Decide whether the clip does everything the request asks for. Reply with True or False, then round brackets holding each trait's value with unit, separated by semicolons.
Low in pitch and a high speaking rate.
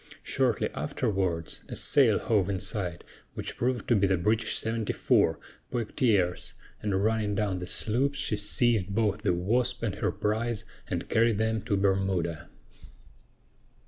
False (105 Hz; 145 wpm)